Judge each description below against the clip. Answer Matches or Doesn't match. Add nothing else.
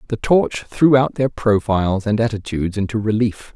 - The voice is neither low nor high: Doesn't match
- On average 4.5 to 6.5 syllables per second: Matches